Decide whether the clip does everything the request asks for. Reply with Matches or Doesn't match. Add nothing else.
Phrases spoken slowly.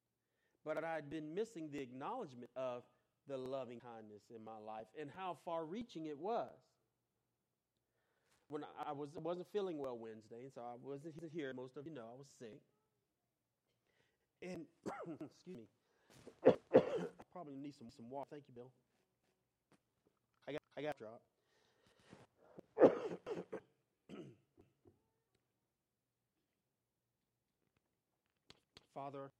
Matches